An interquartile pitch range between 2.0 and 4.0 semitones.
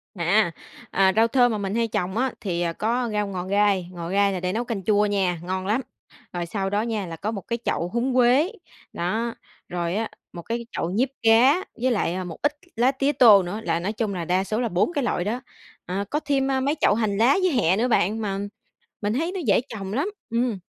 No: average, 4.4 semitones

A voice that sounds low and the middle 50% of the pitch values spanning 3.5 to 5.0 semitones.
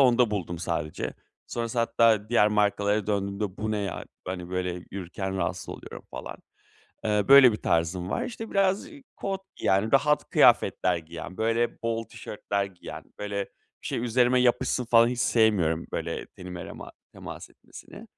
Yes: low, 105 Hz; average, 4.2 semitones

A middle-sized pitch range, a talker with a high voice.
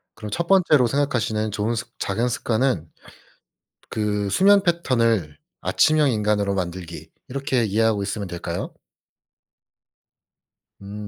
No: average, 4.7 semitones; low, 110 Hz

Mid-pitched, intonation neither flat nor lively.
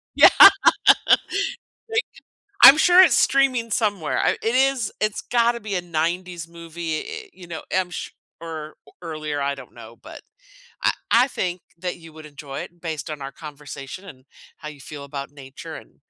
No: medium, 170 Hz; wide, 7.0 semitones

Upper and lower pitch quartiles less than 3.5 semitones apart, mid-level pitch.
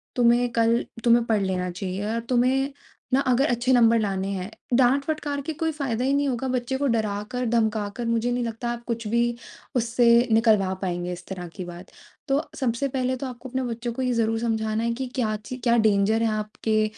No: average, 2.7 semitones; high, 235 Hz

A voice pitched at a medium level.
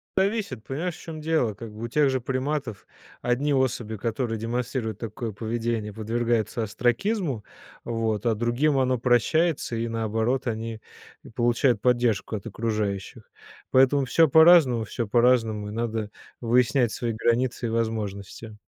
No: low, 120 Hz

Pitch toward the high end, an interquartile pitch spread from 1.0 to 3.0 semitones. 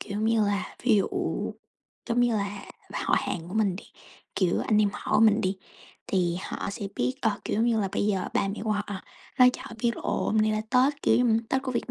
Yes: high, 215 Hz; average, 2.7 semitones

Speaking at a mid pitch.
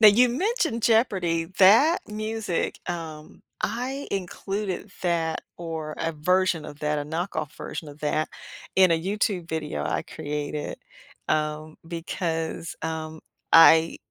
Yes: medium, 165 Hz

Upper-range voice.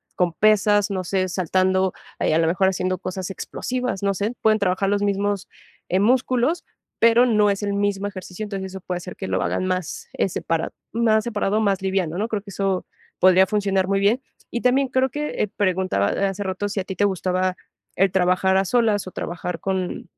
Yes: high, 195 Hz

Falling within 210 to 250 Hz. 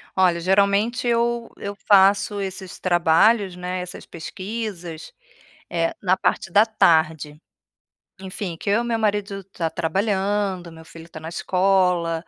No: high, 190 Hz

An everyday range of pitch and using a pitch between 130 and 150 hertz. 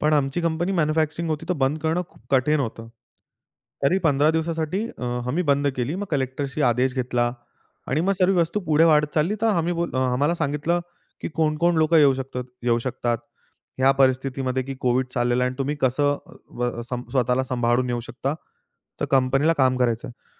Yes: average, 4.0 semitones; medium, 140 Hz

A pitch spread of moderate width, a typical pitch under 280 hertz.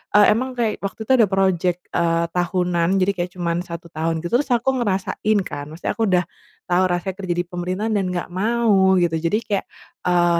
Yes: average, 3.1 semitones; medium, 185 Hz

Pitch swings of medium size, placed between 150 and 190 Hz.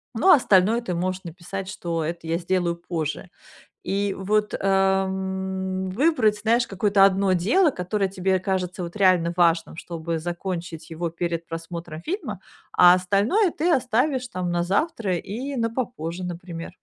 Yes: average, 3.3 semitones; medium, 185 Hz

